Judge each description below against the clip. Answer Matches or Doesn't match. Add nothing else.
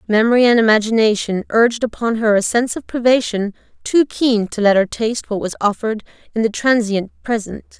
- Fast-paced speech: Doesn't match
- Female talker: Matches